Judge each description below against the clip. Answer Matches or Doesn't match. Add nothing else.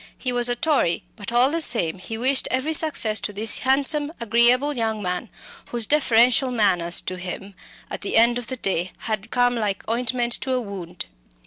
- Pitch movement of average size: Matches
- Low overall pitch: Doesn't match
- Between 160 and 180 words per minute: Doesn't match